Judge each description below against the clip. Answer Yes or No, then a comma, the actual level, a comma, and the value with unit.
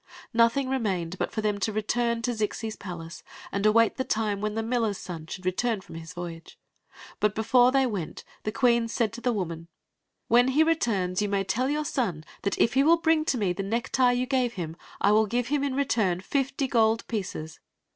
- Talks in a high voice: Yes, high, 225 Hz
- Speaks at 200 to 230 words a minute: Yes, fast, 205 wpm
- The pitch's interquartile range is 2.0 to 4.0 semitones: No, average, 4.4 semitones